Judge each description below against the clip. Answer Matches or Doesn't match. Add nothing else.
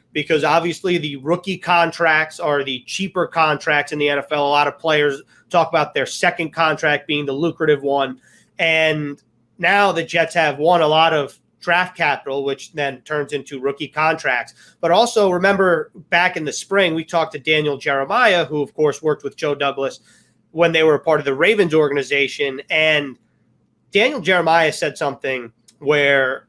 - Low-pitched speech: Doesn't match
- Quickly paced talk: Doesn't match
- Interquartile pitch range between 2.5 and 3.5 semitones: Matches